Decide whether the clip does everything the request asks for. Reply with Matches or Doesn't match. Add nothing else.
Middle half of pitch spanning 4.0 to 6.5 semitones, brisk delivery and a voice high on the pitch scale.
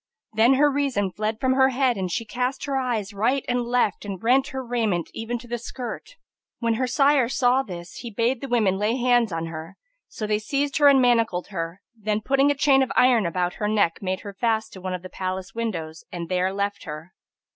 Matches